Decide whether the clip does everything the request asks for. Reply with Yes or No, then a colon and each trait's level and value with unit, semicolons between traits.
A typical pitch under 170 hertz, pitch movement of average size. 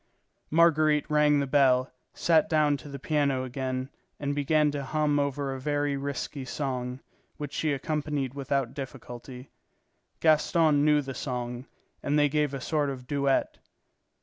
No: medium, 140 Hz; narrow, 2.1 semitones